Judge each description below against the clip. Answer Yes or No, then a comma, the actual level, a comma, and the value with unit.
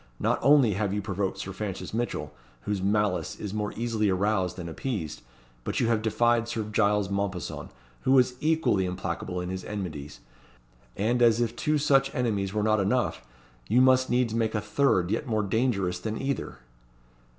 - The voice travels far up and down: No, average, 3.7 semitones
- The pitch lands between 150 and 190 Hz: No, low, 105 Hz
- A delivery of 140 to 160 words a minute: No, average, 175 wpm